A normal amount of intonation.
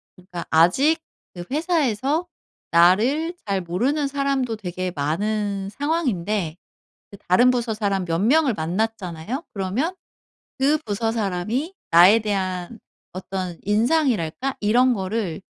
No: wide, 6.3 semitones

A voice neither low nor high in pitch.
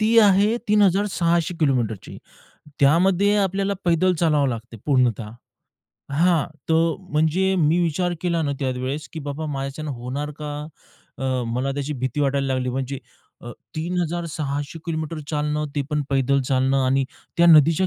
Yes: medium, 150 Hz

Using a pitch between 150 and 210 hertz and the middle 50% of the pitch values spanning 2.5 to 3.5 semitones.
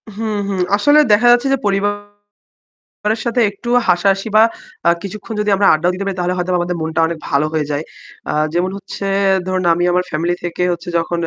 Yes: medium, 185 Hz; average, 2.9 semitones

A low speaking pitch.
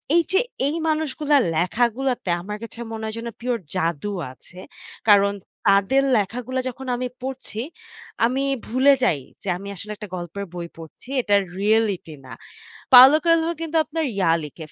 No: high, 225 Hz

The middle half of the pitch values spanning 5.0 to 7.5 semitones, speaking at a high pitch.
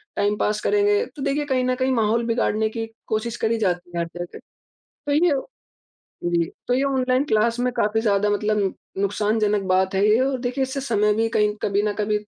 No: average, 3.6 semitones; high, 220 Hz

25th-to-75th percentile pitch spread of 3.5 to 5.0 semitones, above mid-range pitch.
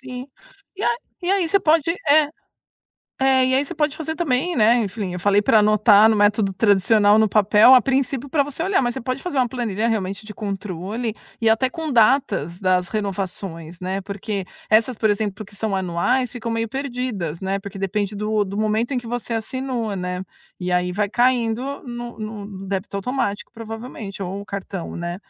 Yes: average, 4.3 semitones; high, 220 Hz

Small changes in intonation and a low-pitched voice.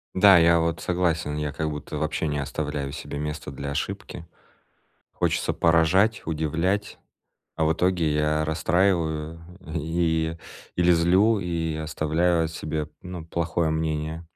Yes: narrow, 2.1 semitones; very low, 80 Hz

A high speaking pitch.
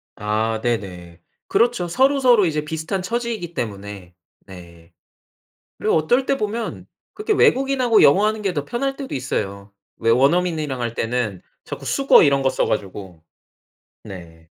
No: medium, 145 Hz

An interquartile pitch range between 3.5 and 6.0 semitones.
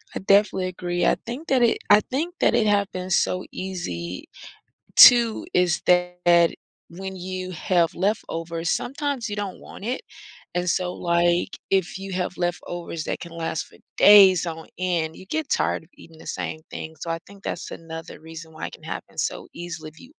No: average, 3.1 semitones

